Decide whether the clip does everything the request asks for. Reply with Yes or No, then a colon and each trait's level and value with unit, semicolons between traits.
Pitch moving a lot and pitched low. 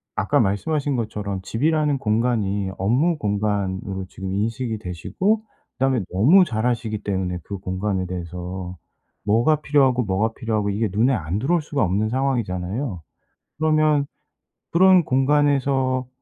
Yes: wide, 6.1 semitones; low, 110 Hz